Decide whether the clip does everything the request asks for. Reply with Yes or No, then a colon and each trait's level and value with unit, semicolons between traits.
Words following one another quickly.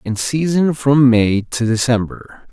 No: average, 145 wpm